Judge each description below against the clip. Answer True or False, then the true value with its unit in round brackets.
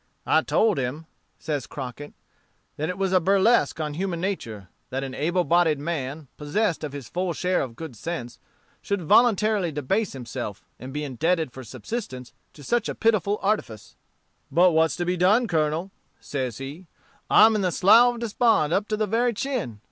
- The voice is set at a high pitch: False (170 Hz)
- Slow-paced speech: False (180 wpm)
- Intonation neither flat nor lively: False (6.1 semitones)